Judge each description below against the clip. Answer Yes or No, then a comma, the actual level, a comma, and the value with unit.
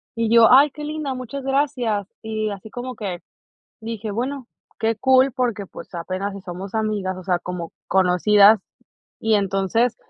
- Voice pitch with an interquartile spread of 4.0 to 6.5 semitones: Yes, average, 4.5 semitones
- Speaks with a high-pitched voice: Yes, high, 220 Hz